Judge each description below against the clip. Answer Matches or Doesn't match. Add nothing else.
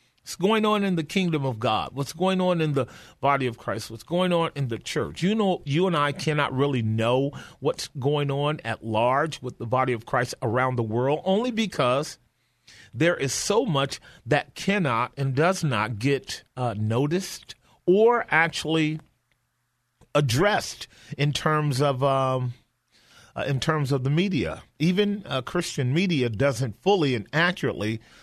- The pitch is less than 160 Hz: Matches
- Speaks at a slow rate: Doesn't match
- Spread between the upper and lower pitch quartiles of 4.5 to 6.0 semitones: Matches